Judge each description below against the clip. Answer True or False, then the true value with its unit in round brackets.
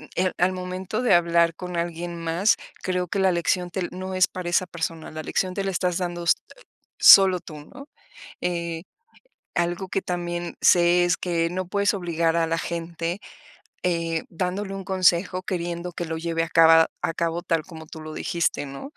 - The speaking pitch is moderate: True (175 Hz)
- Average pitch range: False (1.7 semitones)